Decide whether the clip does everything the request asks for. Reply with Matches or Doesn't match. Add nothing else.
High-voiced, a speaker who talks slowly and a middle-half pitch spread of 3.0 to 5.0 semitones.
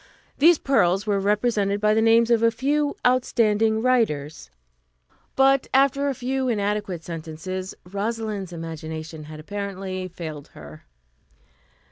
Doesn't match